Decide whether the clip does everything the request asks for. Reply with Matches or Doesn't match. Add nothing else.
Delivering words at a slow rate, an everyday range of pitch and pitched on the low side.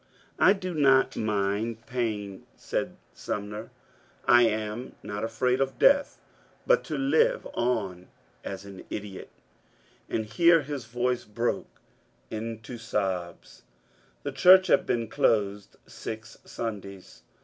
Matches